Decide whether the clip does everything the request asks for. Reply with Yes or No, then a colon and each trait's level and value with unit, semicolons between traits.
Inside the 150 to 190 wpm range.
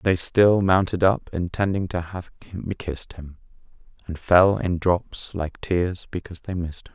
Yes: average, 165 wpm